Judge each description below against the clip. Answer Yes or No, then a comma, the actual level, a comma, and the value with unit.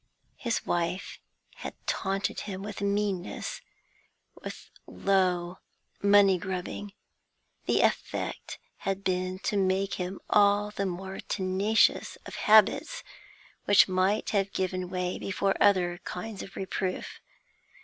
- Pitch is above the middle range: Yes, high, 195 Hz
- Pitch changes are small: Yes, narrow, 1.7 semitones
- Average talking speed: No, slow, 115 wpm